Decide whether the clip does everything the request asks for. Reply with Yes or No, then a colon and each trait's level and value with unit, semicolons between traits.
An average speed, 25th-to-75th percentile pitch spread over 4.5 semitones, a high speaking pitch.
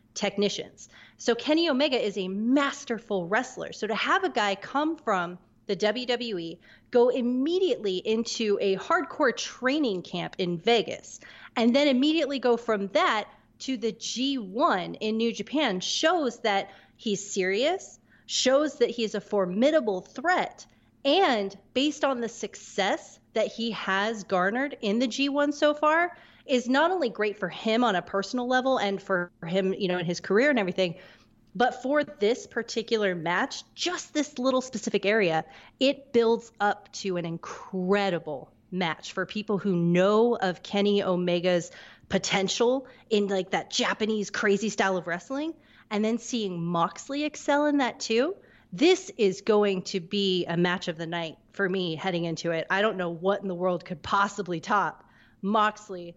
Yes: average, 160 wpm; average, 5.3 semitones; high, 215 Hz